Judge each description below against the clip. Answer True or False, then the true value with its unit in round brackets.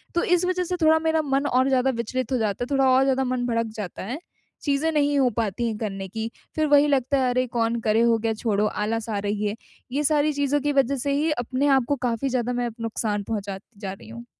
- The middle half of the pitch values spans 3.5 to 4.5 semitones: True (4.1 semitones)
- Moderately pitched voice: False (250 Hz)